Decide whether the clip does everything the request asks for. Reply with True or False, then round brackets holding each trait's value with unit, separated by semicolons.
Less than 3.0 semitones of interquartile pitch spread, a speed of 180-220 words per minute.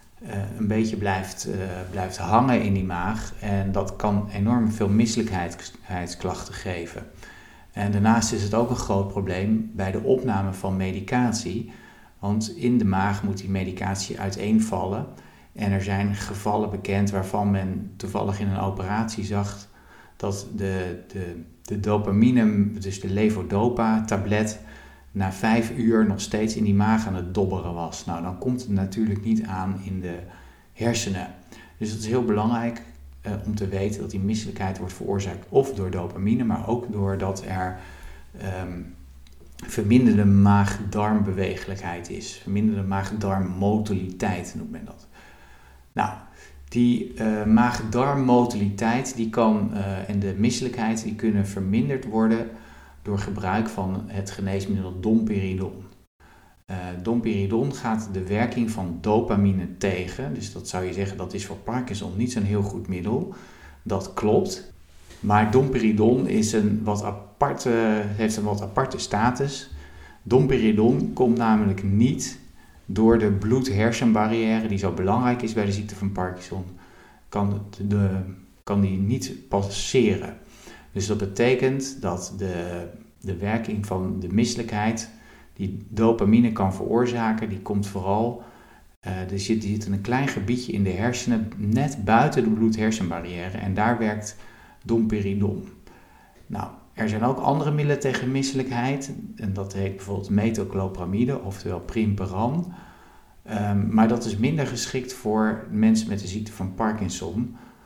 False (2.6 semitones; 140 wpm)